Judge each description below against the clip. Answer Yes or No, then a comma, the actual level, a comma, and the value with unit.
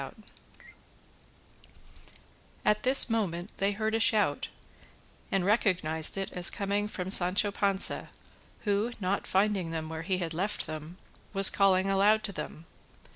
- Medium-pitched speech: No, high, 195 Hz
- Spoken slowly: Yes, slow, 130 wpm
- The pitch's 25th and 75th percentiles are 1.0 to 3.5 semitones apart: Yes, average, 2.9 semitones